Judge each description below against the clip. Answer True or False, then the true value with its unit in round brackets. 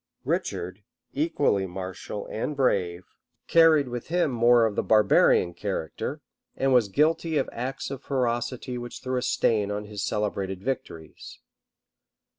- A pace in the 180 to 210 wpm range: False (135 wpm)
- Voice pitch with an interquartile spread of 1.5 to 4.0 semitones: False (5.1 semitones)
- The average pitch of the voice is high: False (120 Hz)